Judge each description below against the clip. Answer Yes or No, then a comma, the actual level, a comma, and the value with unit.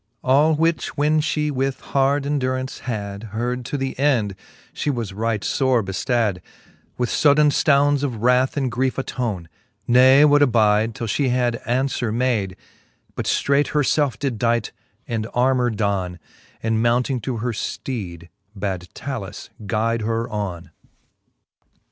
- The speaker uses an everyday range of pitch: Yes, average, 3.9 semitones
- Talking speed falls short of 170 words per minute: Yes, average, 140 wpm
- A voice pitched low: Yes, low, 125 Hz